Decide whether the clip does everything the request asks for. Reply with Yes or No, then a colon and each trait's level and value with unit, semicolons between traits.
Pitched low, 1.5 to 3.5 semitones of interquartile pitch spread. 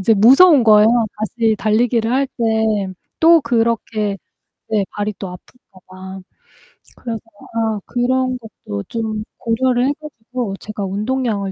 No: high, 225 Hz; average, 2.9 semitones